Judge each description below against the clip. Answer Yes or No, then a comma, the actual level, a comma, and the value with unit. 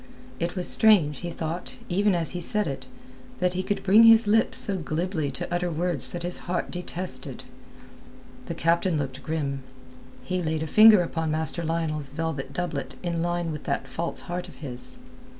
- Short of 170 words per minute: No, average, 180 wpm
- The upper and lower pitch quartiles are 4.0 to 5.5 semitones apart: No, average, 2.8 semitones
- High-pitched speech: No, medium, 170 Hz